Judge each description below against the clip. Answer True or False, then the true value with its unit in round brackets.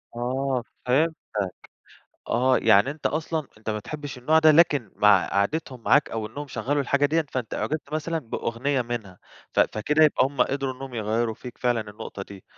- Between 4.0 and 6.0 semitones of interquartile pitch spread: True (4.5 semitones)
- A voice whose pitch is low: True (130 Hz)